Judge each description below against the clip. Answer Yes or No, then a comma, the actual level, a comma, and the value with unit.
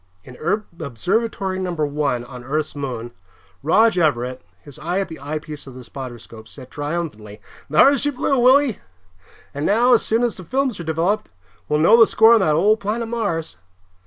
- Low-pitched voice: No, medium, 165 Hz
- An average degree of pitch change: No, wide, 8.0 semitones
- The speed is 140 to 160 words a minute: No, average, 180 wpm